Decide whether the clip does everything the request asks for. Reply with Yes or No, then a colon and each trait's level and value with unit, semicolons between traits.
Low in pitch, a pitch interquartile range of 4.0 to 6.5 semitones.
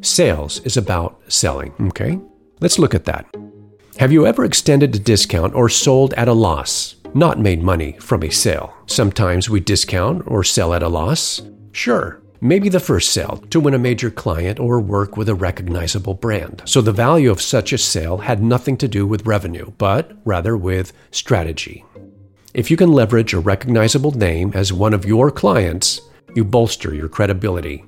Yes: low, 105 Hz; average, 4.4 semitones